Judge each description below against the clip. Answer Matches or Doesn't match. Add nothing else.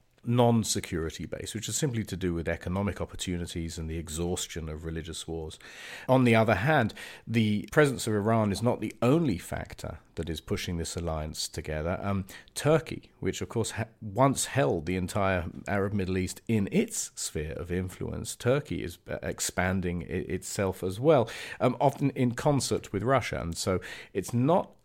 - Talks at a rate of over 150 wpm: Matches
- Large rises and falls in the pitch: Doesn't match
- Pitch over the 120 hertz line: Doesn't match